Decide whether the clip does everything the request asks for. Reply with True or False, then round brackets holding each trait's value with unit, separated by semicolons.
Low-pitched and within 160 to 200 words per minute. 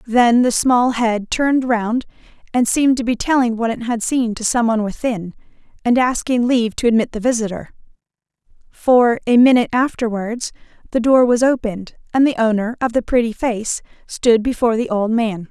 False (235 Hz; 180 wpm)